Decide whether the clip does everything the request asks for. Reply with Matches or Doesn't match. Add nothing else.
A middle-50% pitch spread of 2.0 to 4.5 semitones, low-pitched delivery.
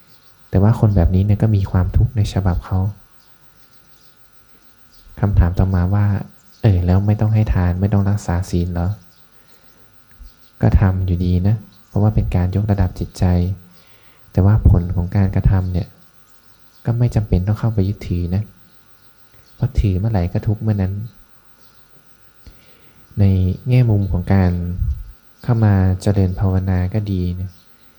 Matches